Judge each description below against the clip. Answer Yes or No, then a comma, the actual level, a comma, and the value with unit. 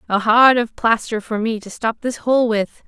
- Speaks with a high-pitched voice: Yes, high, 225 Hz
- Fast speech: Yes, fast, 230 wpm